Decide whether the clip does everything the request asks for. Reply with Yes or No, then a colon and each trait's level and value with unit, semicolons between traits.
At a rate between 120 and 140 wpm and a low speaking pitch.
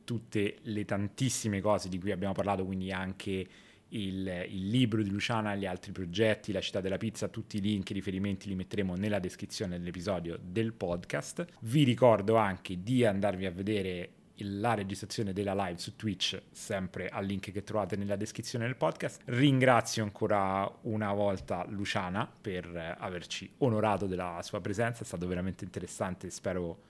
No: average, 165 wpm; low, 100 Hz